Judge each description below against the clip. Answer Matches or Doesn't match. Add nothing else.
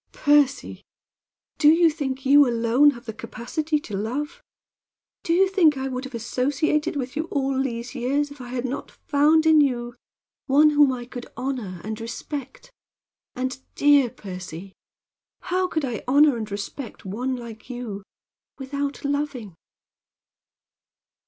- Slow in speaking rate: Doesn't match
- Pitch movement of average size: Matches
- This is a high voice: Matches